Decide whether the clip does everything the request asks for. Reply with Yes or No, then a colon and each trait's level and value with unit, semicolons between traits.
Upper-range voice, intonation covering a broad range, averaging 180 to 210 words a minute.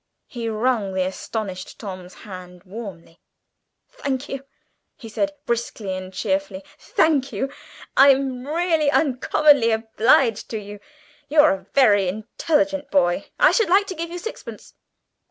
No: high, 235 Hz; wide, 7.0 semitones; slow, 135 wpm